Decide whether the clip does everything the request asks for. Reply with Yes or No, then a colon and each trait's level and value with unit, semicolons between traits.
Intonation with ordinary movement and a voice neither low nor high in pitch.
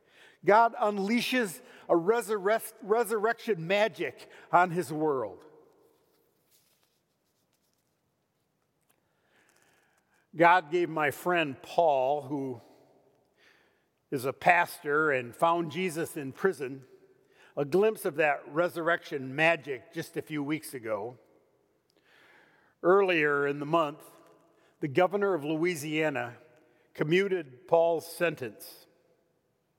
No: wide, 5.8 semitones; medium, 170 Hz